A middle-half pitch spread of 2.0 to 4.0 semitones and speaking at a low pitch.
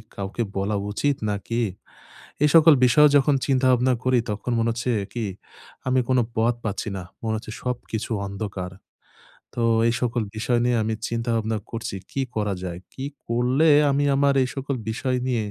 Yes: average, 2.8 semitones; low, 120 Hz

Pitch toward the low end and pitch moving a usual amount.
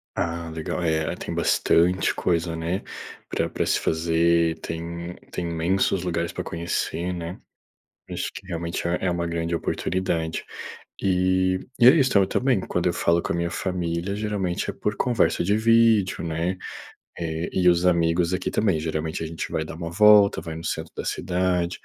No: very low, 85 Hz; narrow, 1.9 semitones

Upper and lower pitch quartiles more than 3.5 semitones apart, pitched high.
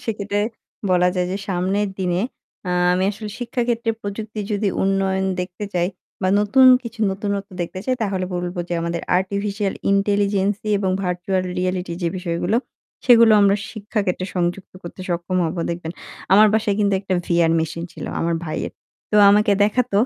No: narrow, 2.6 semitones; high, 195 Hz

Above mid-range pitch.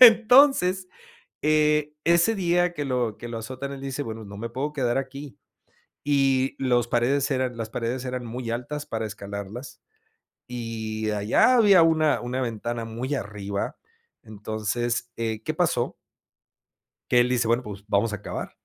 No: low, 125 Hz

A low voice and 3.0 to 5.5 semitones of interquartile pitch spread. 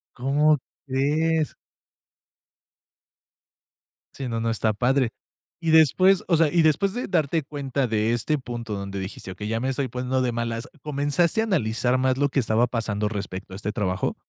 Yes: low, 130 Hz; average, 5.0 semitones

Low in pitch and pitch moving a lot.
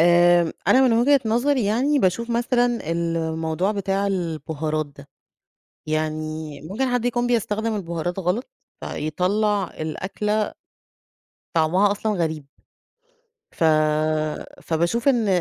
No: high, 195 Hz; wide, 6.1 semitones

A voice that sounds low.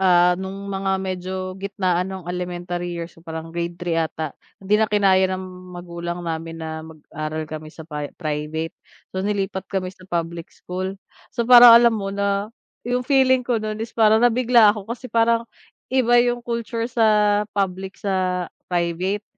No: high, 190 Hz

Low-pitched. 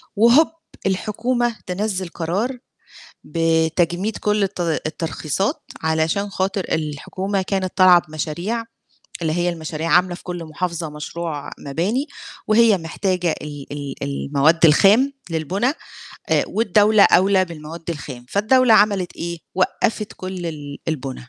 No: medium, 175 Hz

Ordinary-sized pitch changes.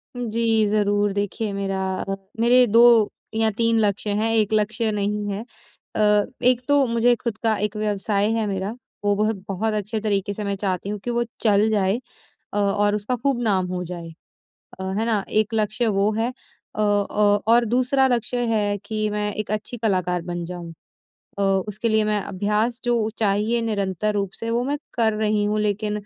No: narrow, 1.9 semitones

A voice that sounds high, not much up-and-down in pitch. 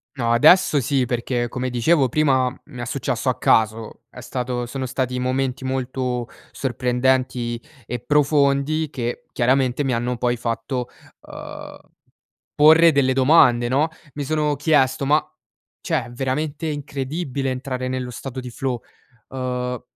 No: low, 130 Hz; narrow, 2.2 semitones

